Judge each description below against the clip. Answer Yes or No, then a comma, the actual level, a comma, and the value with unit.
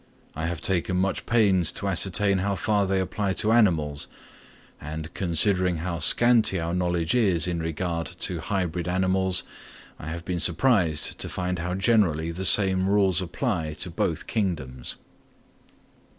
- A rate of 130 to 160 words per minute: Yes, average, 150 wpm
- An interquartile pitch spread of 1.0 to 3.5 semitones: Yes, average, 2.7 semitones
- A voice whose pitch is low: Yes, very low, 90 Hz